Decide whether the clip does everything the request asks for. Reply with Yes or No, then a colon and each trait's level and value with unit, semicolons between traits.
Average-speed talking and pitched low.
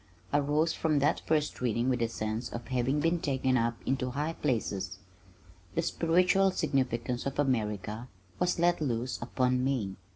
Yes: average, 160 wpm; low, 130 Hz